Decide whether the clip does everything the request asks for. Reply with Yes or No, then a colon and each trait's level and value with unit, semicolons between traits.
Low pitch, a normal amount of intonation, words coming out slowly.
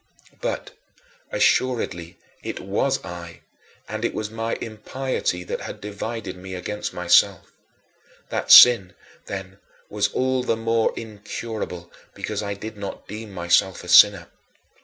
Yes: low, 105 Hz; average, 3.4 semitones; slow, 130 wpm